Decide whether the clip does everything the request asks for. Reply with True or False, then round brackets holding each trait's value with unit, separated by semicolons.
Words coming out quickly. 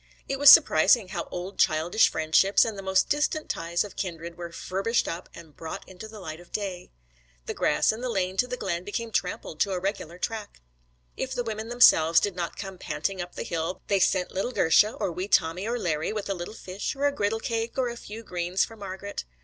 True (230 wpm)